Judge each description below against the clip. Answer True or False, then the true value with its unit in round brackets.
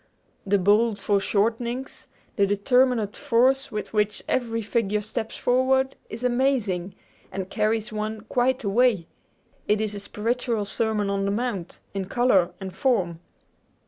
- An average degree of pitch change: True (3.5 semitones)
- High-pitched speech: True (220 Hz)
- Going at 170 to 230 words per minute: False (135 wpm)